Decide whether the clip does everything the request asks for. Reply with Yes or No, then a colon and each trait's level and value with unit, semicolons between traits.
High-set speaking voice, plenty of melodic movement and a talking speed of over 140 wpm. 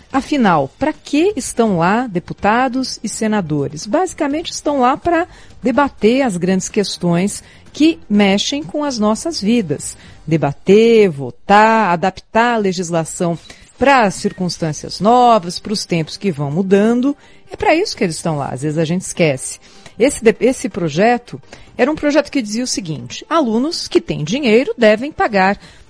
Yes: high, 215 Hz; wide, 6.9 semitones; average, 150 wpm